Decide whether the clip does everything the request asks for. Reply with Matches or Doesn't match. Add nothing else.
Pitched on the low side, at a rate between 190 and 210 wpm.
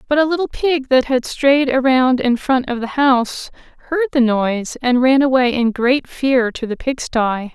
Doesn't match